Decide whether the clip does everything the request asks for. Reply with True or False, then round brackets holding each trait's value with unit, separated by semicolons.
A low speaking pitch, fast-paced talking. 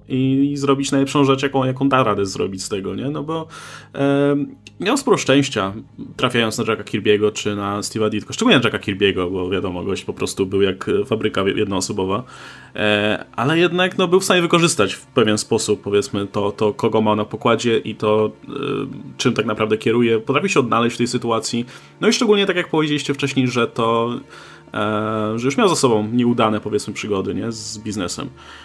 True (115 Hz; 195 wpm)